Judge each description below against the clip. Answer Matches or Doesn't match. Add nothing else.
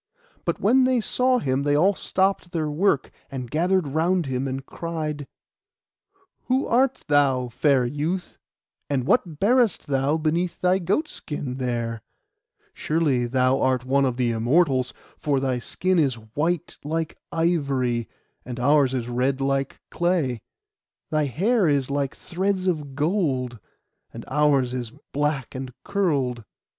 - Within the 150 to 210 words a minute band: Doesn't match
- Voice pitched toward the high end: Doesn't match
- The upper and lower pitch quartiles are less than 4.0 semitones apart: Doesn't match